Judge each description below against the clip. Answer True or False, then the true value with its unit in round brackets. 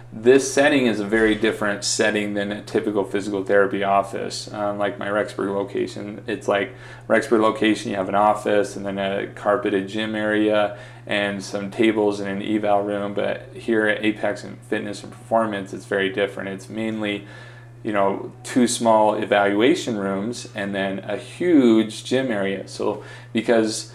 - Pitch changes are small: True (2.0 semitones)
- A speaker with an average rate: True (165 wpm)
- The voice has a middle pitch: False (105 Hz)